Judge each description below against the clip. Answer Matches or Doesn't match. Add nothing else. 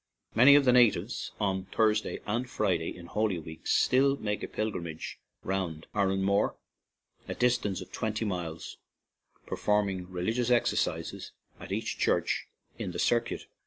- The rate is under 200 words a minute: Matches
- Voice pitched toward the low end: Matches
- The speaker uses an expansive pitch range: Doesn't match